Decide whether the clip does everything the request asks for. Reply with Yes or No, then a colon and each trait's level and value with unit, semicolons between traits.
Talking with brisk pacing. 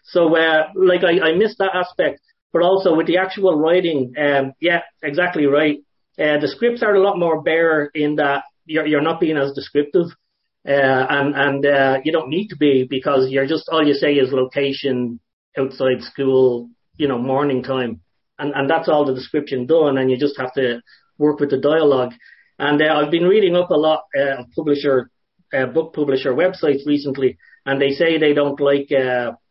No: average, 195 wpm